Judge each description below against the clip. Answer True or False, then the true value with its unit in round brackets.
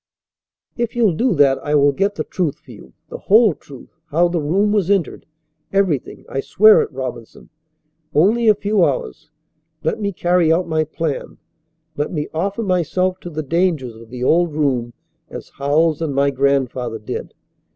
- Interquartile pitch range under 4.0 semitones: False (5.3 semitones)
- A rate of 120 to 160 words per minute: False (170 wpm)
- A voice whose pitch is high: False (160 Hz)